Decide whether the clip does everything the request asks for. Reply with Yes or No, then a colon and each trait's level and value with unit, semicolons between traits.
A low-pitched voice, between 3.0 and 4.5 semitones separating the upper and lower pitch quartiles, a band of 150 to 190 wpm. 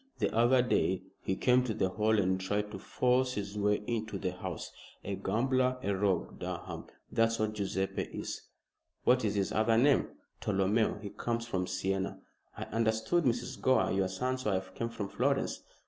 Yes: low, 105 Hz; average, 3.7 semitones; average, 175 wpm